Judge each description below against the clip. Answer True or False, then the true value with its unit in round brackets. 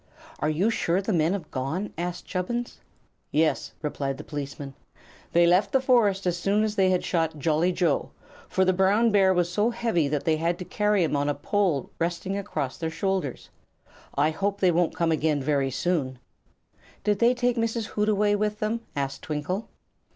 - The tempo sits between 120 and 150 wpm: False (185 wpm)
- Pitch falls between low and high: True (180 Hz)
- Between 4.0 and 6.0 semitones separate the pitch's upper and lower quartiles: True (4.9 semitones)